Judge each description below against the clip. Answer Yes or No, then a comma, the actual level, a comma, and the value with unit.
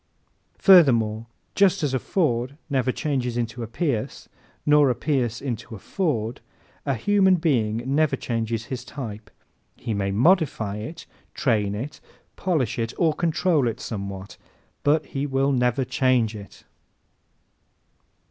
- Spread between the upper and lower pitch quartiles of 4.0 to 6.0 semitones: Yes, average, 4.9 semitones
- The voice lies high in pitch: No, low, 125 Hz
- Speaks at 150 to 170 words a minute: No, slow, 135 wpm